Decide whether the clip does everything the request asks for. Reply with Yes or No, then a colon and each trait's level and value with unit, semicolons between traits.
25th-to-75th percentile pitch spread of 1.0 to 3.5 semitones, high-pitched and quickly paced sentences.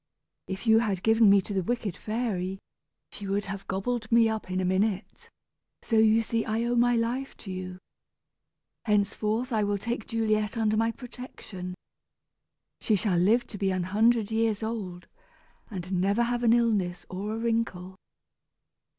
No: average, 3.1 semitones; high, 215 Hz; average, 165 wpm